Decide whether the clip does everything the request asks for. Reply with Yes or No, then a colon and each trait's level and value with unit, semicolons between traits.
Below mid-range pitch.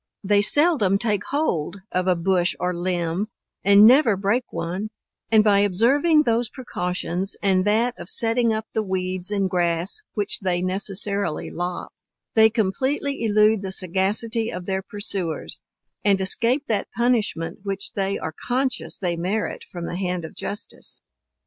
No: high, 200 Hz